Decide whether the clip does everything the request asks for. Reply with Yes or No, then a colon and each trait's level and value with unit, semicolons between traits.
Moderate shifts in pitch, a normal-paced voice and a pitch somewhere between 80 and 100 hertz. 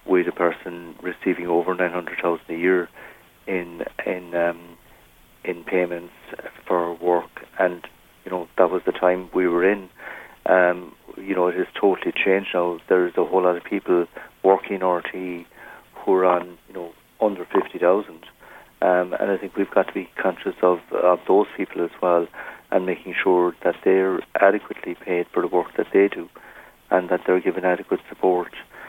No: narrow, 1.0 semitones; average, 170 wpm; very low, 90 Hz